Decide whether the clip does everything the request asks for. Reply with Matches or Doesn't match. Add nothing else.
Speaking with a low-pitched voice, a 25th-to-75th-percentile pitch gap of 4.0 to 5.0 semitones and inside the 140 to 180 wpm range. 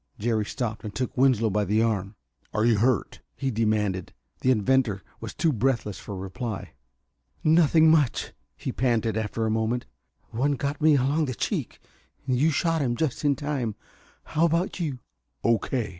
Matches